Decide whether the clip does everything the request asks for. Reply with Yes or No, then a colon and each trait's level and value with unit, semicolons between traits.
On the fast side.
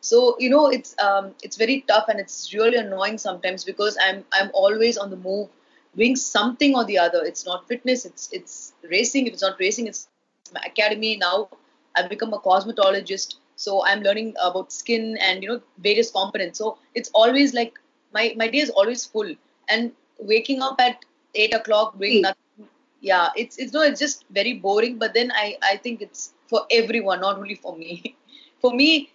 Yes: fast, 195 wpm